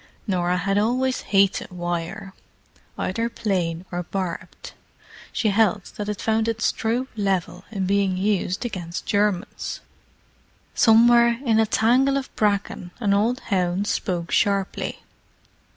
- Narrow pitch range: No, average, 3.4 semitones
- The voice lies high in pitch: Yes, high, 200 Hz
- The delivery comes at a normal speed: No, slow, 125 wpm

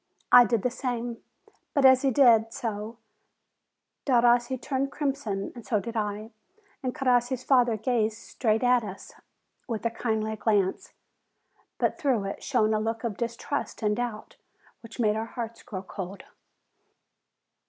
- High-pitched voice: Yes, high, 230 Hz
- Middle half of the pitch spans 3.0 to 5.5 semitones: No, narrow, 2.4 semitones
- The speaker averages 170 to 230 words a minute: No, average, 145 wpm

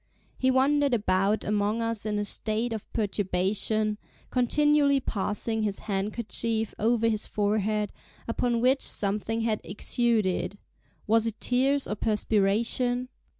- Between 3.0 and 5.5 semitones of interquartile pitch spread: No, narrow, 2.5 semitones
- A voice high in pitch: Yes, high, 220 Hz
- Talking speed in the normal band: No, slow, 115 wpm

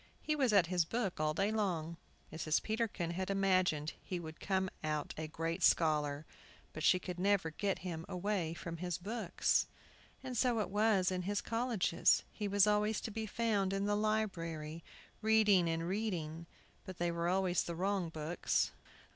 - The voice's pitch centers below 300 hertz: Yes, medium, 185 Hz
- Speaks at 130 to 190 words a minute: Yes, average, 170 wpm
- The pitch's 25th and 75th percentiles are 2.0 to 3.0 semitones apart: No, average, 3.9 semitones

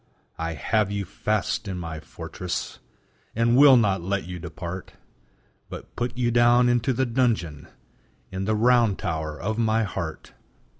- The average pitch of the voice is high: No, low, 100 Hz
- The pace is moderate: Yes, average, 150 wpm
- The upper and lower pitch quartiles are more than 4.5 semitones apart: Yes, wide, 5.6 semitones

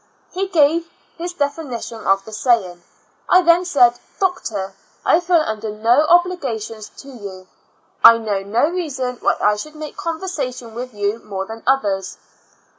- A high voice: Yes, high, 245 Hz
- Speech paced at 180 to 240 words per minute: No, average, 150 wpm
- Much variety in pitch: Yes, wide, 7.4 semitones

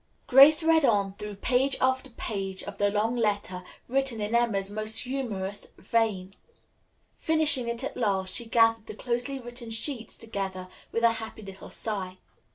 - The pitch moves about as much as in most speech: Yes, average, 3.7 semitones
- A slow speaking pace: No, average, 160 wpm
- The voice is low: No, high, 225 Hz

